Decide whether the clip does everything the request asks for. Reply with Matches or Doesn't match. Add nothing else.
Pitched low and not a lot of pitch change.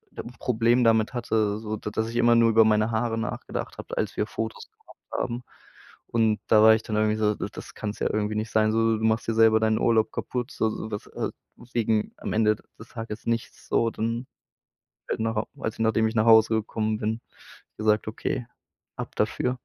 Matches